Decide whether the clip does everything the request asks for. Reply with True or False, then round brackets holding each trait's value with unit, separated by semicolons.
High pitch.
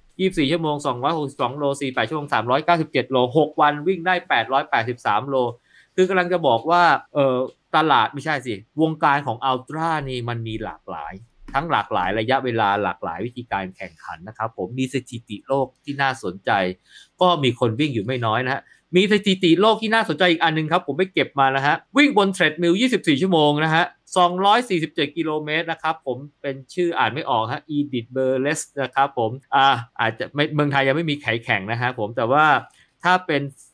False (140 Hz)